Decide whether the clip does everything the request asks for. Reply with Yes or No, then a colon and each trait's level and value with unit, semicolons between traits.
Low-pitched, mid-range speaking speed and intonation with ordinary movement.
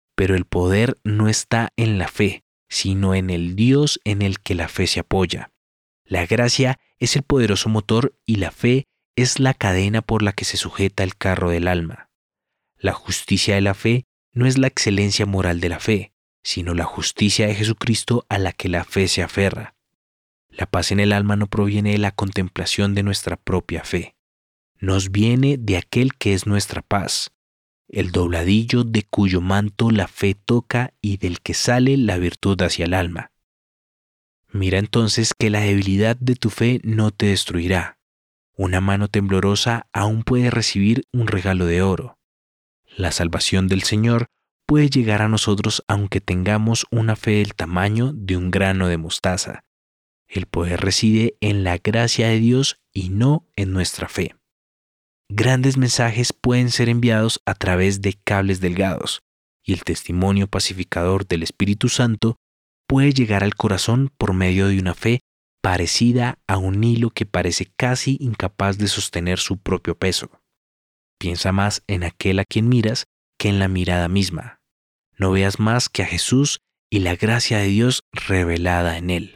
Yes: low, 100 Hz; average, 170 wpm; average, 3.6 semitones